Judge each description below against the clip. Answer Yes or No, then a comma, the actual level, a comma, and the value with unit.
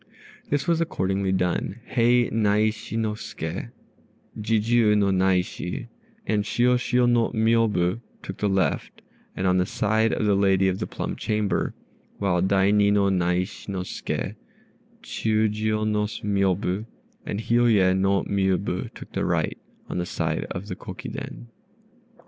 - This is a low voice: Yes, low, 100 Hz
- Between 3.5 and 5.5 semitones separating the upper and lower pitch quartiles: No, narrow, 2.6 semitones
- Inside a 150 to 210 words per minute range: No, slow, 135 wpm